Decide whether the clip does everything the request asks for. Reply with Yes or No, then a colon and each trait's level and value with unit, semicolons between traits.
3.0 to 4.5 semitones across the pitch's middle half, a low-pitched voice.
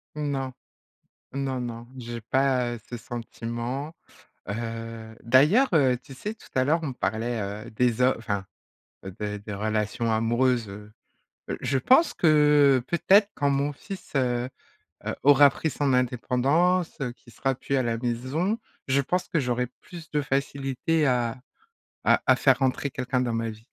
Yes: average, 3.4 semitones; low, 130 Hz